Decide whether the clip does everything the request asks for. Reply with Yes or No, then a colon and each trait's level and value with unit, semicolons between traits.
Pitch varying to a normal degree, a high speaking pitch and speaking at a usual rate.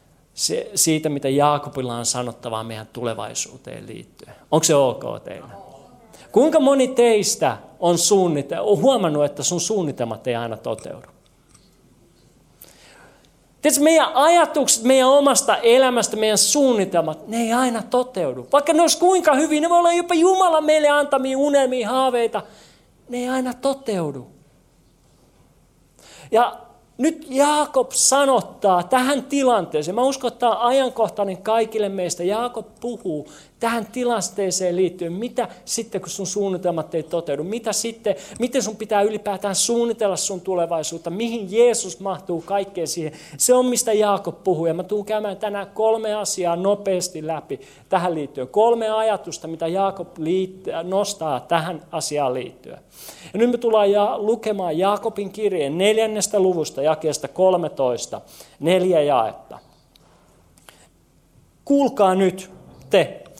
No: wide, 6.1 semitones; high, 205 Hz; average, 130 wpm